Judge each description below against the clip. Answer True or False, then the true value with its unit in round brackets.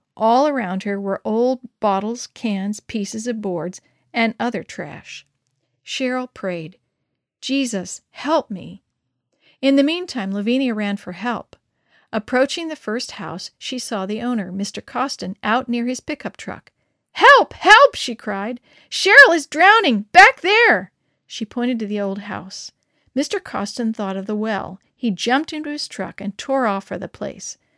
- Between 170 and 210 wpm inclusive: False (160 wpm)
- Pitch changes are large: False (4.7 semitones)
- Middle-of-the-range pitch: False (235 Hz)